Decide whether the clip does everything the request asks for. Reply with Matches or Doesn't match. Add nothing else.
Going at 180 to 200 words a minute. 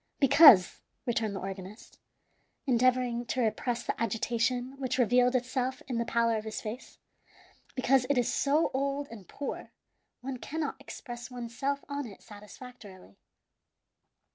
Doesn't match